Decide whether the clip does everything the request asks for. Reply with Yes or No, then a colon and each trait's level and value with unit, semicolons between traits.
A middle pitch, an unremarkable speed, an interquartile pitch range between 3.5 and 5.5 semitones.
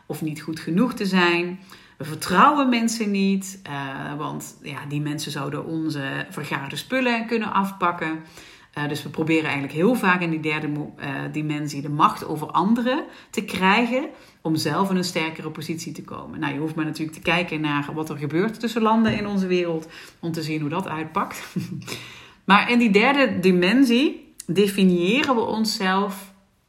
Yes: medium, 175 Hz; average, 165 wpm; average, 5.1 semitones